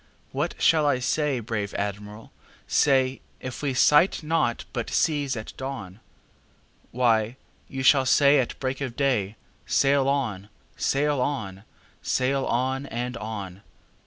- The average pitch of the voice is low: Yes, low, 130 Hz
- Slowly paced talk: Yes, slow, 120 wpm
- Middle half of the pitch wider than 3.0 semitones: Yes, average, 4.1 semitones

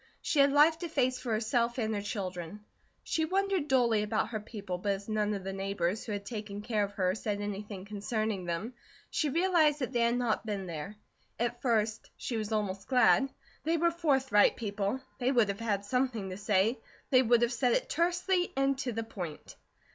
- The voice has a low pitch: No, high, 220 Hz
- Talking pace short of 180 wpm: No, average, 200 wpm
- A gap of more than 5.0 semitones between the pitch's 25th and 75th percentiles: No, average, 4.3 semitones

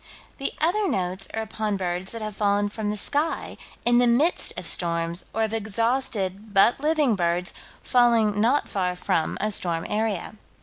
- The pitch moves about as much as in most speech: Yes, average, 4.0 semitones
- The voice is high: Yes, high, 215 Hz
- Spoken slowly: No, average, 170 wpm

